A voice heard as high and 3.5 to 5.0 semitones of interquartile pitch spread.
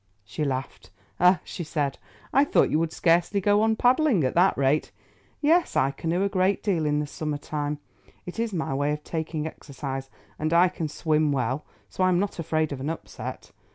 No: medium, 160 Hz; average, 4.0 semitones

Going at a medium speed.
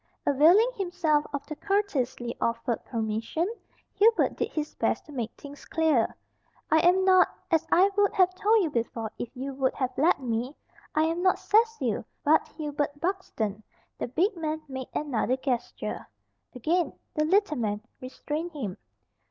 Yes: average, 155 wpm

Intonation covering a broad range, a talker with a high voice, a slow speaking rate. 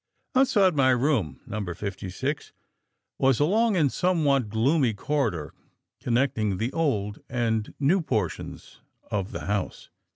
No: wide, 6.3 semitones; low, 130 Hz; slow, 125 wpm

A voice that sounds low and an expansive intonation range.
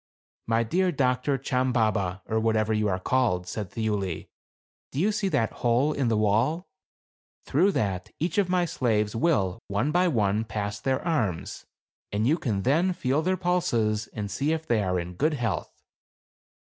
Yes: low, 115 Hz; wide, 6.6 semitones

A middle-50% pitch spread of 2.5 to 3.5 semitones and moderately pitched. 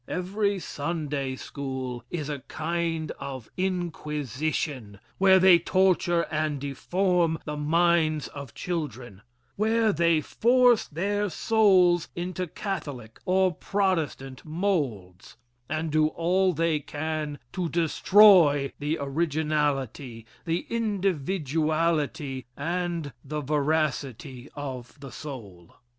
No: average, 4.2 semitones; medium, 155 Hz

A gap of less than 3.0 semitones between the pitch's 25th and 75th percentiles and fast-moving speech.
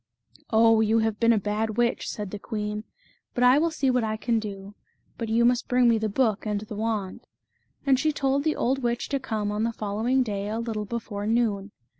Yes: narrow, 2.5 semitones; fast, 230 wpm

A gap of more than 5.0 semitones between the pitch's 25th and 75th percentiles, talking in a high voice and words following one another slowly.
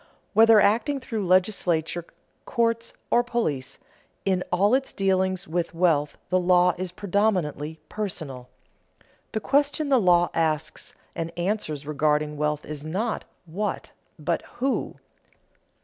No: wide, 5.6 semitones; medium, 180 Hz; slow, 120 wpm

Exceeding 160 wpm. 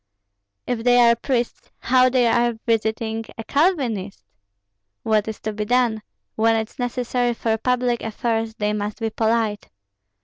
No: average, 145 wpm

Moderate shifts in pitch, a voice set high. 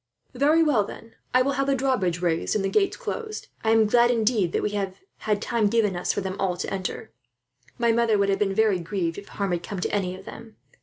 Yes: average, 3.9 semitones; high, 210 Hz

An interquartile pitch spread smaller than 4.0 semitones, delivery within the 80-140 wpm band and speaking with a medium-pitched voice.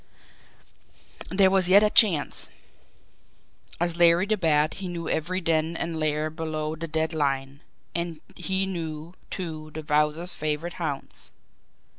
Yes: narrow, 2.4 semitones; slow, 135 wpm; medium, 165 Hz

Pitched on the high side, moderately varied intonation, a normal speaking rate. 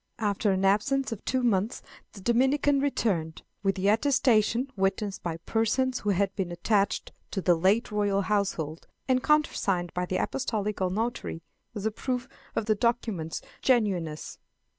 Yes: high, 210 Hz; average, 4.2 semitones; average, 150 wpm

